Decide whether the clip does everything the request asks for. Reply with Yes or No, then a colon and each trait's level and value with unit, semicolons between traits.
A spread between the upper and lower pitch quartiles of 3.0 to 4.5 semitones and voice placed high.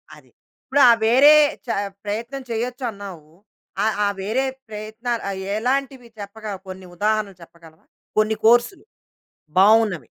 Yes: average, 3.3 semitones; high, 220 Hz